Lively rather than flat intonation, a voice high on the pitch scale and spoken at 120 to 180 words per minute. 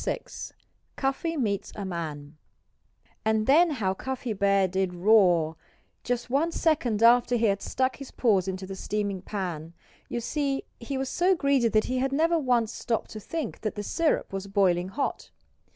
Yes: wide, 5.7 semitones; high, 220 Hz; average, 170 wpm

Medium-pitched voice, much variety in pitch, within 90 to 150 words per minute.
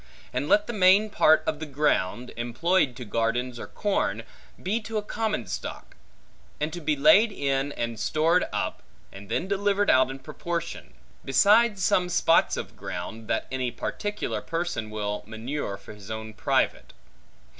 No: medium, 150 Hz; wide, 8.3 semitones; average, 160 wpm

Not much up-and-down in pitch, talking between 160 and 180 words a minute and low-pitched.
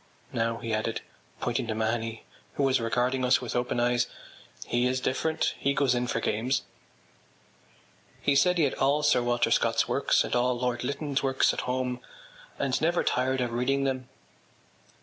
Yes: narrow, 2.0 semitones; average, 170 wpm; low, 125 Hz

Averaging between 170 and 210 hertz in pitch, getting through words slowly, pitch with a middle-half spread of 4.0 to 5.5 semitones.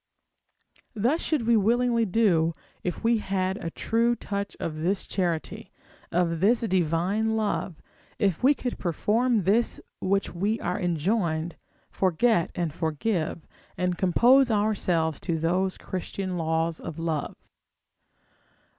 Yes: high, 190 Hz; slow, 125 wpm; average, 5.0 semitones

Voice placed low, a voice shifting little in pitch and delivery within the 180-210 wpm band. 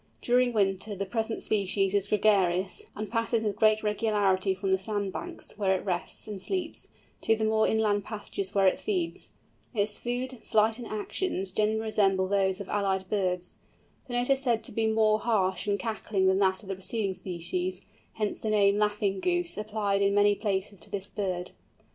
No: high, 205 Hz; narrow, 2.3 semitones; average, 185 wpm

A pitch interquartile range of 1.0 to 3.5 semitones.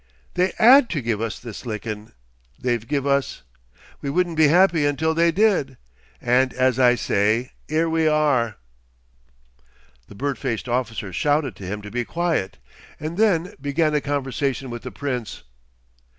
No: average, 5.2 semitones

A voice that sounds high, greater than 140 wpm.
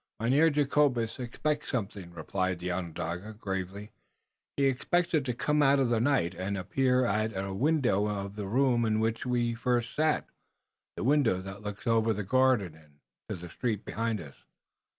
No: low, 115 Hz; average, 170 wpm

